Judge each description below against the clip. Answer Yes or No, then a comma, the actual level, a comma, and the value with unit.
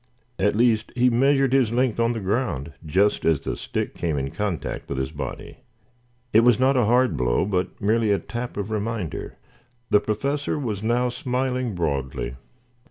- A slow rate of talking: No, average, 170 wpm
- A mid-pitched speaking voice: No, low, 110 Hz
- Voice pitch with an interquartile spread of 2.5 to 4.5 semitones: No, wide, 5.4 semitones